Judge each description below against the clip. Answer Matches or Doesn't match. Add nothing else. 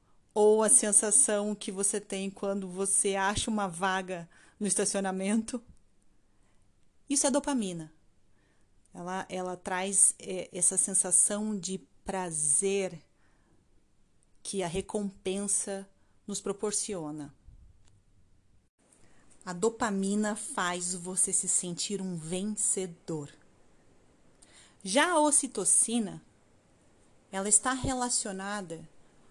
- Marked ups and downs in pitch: Doesn't match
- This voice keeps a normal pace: Doesn't match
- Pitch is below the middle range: Doesn't match